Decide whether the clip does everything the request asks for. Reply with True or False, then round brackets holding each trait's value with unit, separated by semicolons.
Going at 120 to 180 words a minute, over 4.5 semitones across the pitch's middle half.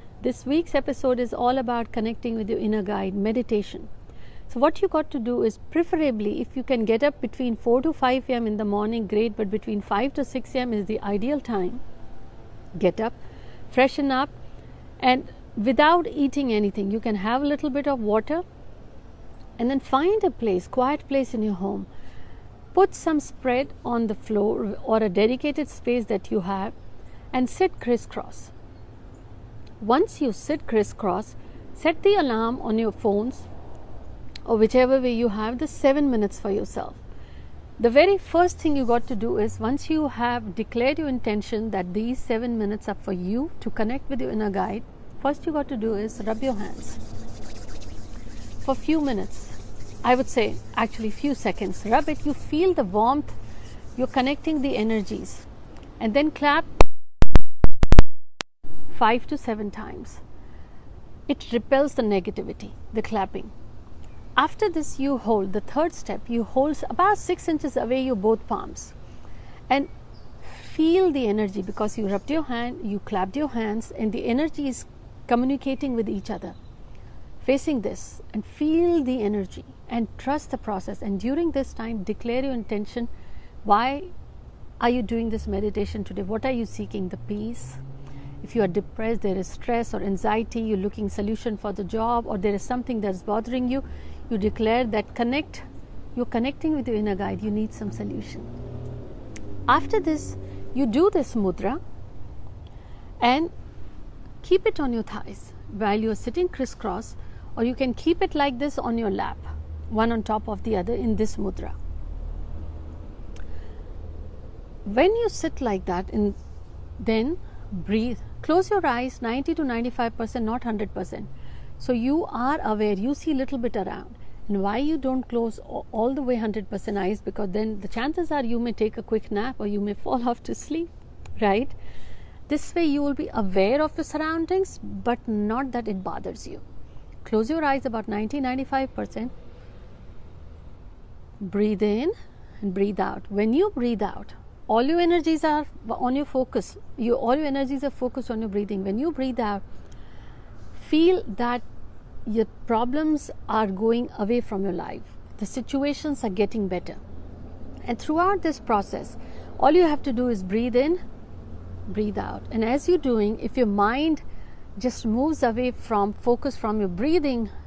True (165 wpm; 4.9 semitones)